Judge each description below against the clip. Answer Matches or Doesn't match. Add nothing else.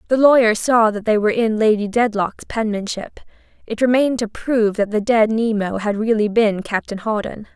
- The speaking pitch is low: Doesn't match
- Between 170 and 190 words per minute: Matches